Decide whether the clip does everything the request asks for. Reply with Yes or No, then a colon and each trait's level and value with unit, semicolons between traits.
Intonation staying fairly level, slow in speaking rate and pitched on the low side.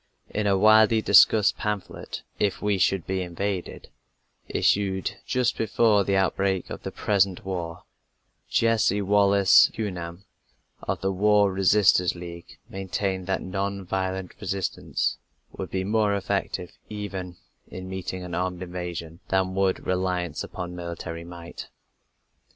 Yes: narrow, 2.0 semitones; slow, 130 wpm; very low, 95 Hz